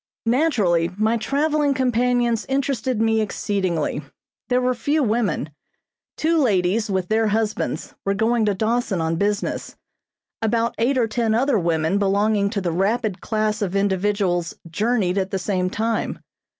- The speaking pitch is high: Yes, high, 215 Hz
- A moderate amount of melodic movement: Yes, average, 3.7 semitones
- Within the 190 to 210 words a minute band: No, average, 145 wpm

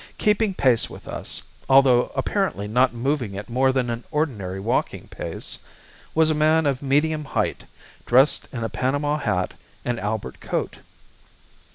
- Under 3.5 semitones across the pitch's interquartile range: No, average, 4.4 semitones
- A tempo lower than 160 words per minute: Yes, average, 150 wpm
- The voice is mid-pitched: No, low, 130 Hz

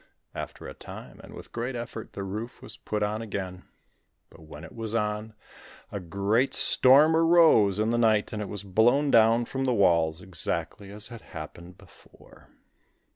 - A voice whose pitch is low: Yes, low, 110 Hz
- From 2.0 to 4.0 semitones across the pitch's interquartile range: Yes, average, 3.3 semitones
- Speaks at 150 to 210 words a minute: Yes, average, 175 wpm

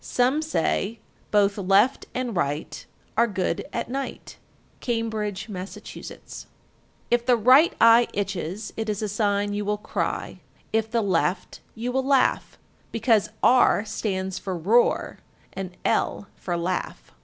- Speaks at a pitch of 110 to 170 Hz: No, high, 210 Hz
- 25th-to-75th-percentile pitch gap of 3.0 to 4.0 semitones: Yes, average, 3.5 semitones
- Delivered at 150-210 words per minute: No, average, 140 wpm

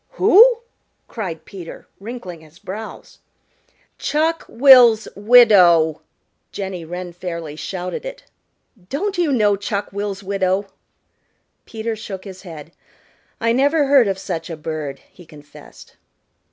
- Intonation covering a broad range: Yes, wide, 6.0 semitones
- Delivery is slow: Yes, slow, 120 wpm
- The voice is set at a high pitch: Yes, high, 200 Hz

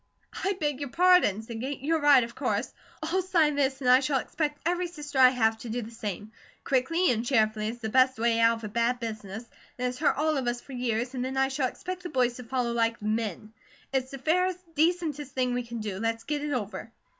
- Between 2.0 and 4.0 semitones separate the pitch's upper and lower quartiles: No, average, 4.4 semitones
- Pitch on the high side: Yes, very high, 255 Hz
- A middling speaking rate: No, fast, 235 wpm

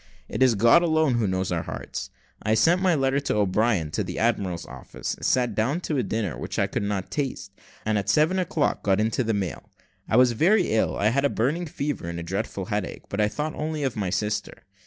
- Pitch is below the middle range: Yes, low, 110 Hz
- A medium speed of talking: No, fast, 225 wpm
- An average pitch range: No, wide, 6.2 semitones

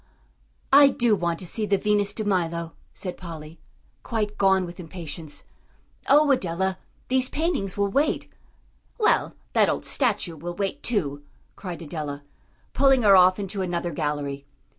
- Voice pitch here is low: No, medium, 185 Hz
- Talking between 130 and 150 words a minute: Yes, average, 145 wpm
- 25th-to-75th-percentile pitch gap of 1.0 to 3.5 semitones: No, average, 4.0 semitones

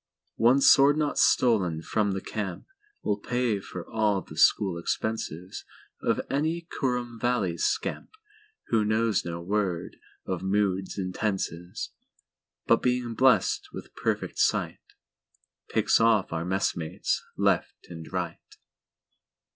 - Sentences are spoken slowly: Yes, slow, 105 wpm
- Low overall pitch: Yes, low, 105 Hz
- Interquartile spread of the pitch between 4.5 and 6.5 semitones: Yes, average, 5.2 semitones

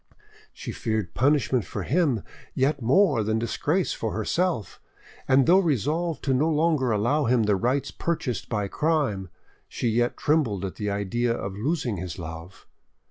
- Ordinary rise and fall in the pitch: No, wide, 6.5 semitones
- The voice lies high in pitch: No, low, 120 Hz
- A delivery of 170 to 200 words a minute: No, average, 155 wpm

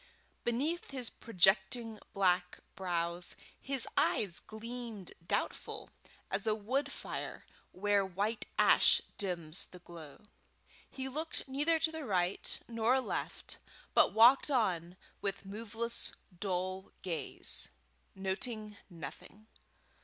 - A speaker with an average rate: No, slow, 105 wpm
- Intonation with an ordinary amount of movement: Yes, average, 4.6 semitones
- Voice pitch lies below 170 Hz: No, high, 205 Hz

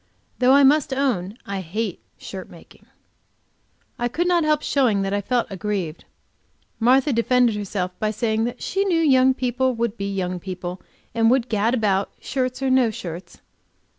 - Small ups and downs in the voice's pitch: No, average, 4.7 semitones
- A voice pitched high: Yes, high, 230 Hz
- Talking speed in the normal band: Yes, average, 165 wpm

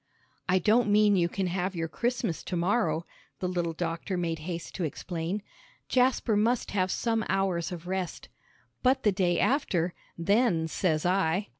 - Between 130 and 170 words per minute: Yes, average, 160 wpm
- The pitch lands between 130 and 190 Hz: Yes, medium, 185 Hz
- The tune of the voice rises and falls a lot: No, average, 3.5 semitones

